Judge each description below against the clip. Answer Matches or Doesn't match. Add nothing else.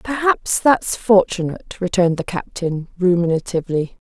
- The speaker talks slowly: Matches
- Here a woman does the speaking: Matches